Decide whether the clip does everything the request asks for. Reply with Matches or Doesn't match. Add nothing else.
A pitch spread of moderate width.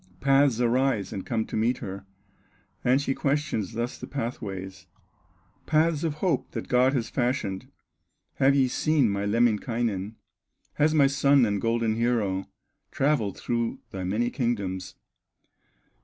Matches